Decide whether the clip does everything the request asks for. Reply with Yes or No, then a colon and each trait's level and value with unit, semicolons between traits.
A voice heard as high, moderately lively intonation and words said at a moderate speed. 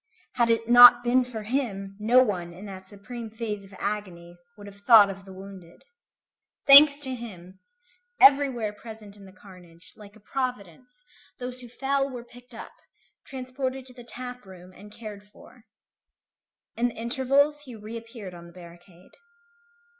Yes: high, 225 Hz; average, 4.2 semitones; average, 160 wpm